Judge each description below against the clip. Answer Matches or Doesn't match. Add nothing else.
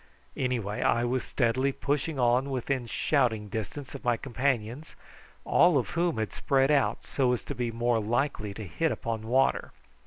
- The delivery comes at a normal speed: Matches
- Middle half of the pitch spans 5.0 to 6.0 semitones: Doesn't match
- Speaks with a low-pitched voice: Matches